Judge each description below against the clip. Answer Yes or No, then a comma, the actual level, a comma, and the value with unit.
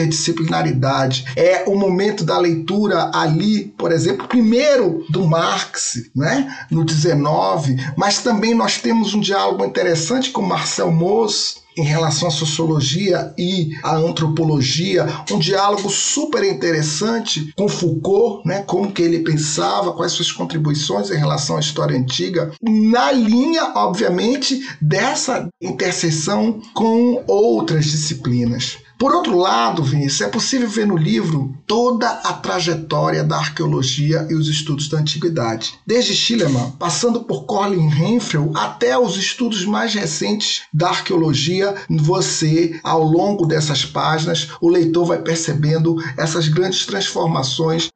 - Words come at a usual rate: Yes, average, 130 wpm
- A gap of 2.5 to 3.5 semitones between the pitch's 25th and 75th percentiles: No, average, 4.5 semitones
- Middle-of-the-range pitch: Yes, medium, 170 Hz